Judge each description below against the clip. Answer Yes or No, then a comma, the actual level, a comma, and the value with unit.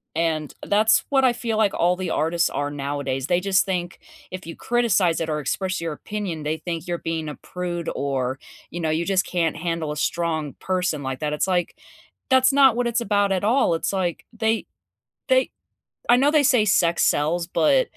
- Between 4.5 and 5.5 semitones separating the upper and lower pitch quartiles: Yes, average, 4.9 semitones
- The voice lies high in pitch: No, medium, 175 Hz